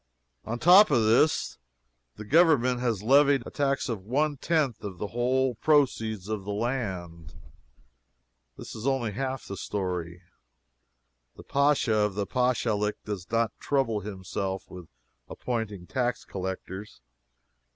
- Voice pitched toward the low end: Yes, low, 115 Hz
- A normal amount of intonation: Yes, average, 4.9 semitones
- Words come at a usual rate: No, slow, 130 wpm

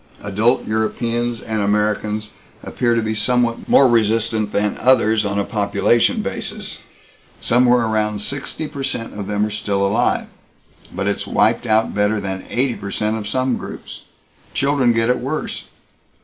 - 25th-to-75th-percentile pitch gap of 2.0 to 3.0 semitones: Yes, narrow, 2.6 semitones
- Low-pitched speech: Yes, low, 110 Hz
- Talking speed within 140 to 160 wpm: Yes, average, 155 wpm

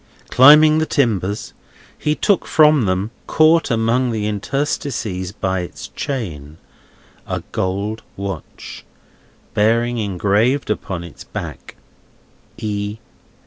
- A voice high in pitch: No, low, 110 Hz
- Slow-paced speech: Yes, slow, 100 wpm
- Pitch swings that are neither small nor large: No, wide, 5.7 semitones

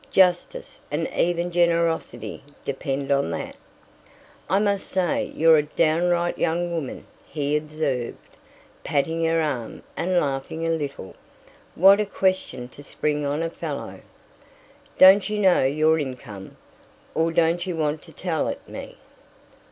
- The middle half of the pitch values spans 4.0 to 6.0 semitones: No, average, 3.4 semitones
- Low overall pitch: No, medium, 160 Hz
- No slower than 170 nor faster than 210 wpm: No, slow, 135 wpm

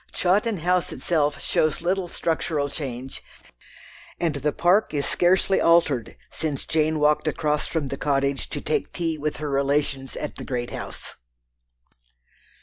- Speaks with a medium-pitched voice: Yes, medium, 150 Hz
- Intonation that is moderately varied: Yes, average, 3.4 semitones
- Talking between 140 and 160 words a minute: Yes, average, 145 wpm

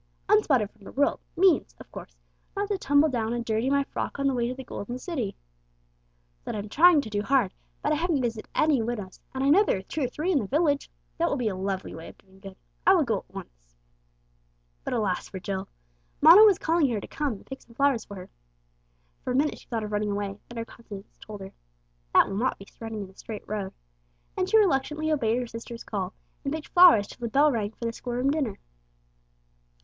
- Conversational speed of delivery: No, fast, 235 wpm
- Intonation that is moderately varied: No, wide, 5.8 semitones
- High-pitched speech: Yes, high, 240 Hz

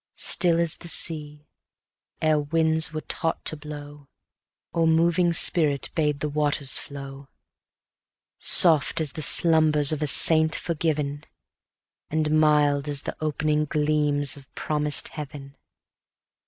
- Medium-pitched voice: Yes, medium, 150 Hz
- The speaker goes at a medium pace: No, slow, 120 wpm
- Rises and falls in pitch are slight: Yes, narrow, 1.6 semitones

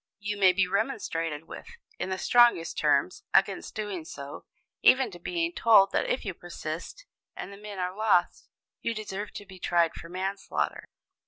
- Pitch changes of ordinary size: Yes, average, 3.6 semitones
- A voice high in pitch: Yes, high, 195 Hz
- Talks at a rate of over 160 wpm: Yes, average, 170 wpm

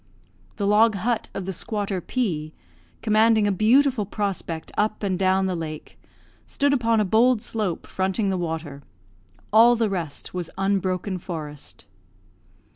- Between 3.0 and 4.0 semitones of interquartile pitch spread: Yes, average, 3.6 semitones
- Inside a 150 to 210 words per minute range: No, average, 140 wpm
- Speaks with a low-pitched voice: No, high, 195 Hz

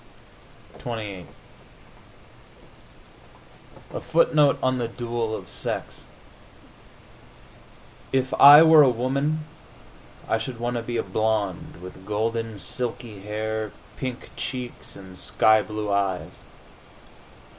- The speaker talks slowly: Yes, slow, 100 wpm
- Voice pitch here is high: No, low, 115 Hz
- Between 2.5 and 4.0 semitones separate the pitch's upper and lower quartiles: Yes, average, 3.3 semitones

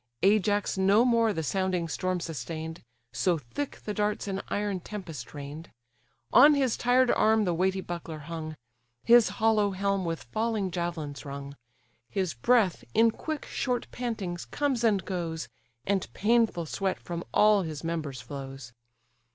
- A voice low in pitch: No, high, 190 Hz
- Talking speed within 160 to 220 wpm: No, average, 145 wpm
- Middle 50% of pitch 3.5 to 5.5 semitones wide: Yes, average, 5.0 semitones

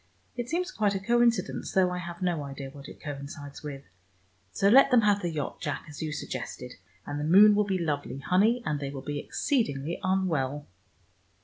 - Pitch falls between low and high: Yes, medium, 170 Hz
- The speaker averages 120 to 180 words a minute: No, average, 195 wpm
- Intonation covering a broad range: Yes, wide, 6.1 semitones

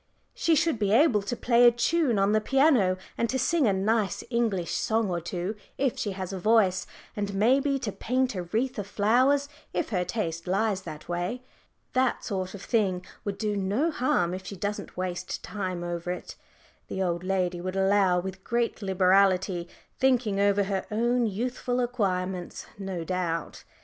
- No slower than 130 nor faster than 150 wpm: No, average, 175 wpm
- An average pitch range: Yes, average, 4.3 semitones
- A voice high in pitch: Yes, high, 200 Hz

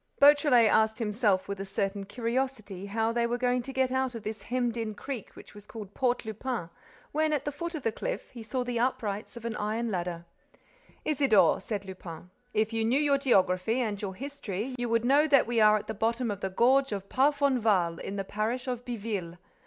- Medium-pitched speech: No, high, 230 Hz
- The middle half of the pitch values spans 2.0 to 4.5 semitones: Yes, average, 3.9 semitones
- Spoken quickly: Yes, fast, 210 wpm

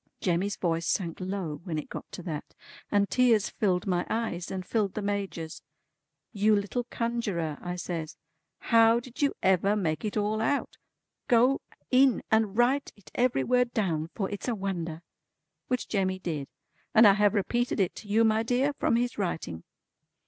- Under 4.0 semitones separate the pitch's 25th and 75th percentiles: No, average, 4.6 semitones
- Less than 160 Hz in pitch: No, high, 205 Hz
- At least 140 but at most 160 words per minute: No, average, 170 wpm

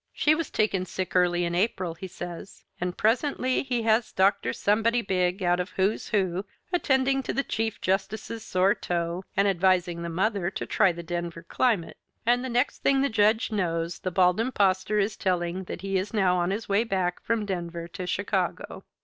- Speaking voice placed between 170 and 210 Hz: Yes, high, 190 Hz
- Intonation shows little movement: No, average, 3.9 semitones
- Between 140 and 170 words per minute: No, average, 190 wpm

